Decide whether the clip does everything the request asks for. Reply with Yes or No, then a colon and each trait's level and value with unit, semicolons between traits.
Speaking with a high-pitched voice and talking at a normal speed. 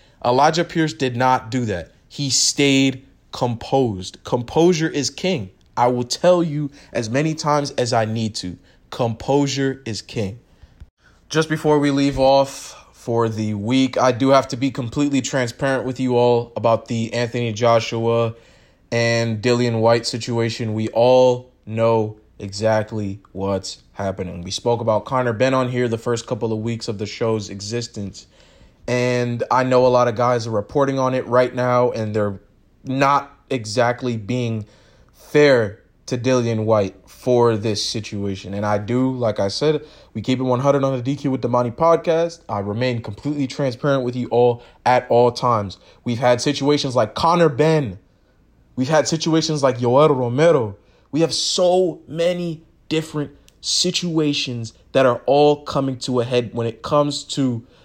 No: low, 125 Hz; average, 160 wpm